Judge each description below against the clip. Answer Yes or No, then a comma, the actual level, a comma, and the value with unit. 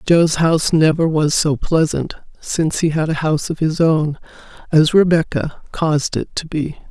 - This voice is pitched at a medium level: Yes, medium, 155 Hz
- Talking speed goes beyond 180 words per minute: No, average, 175 wpm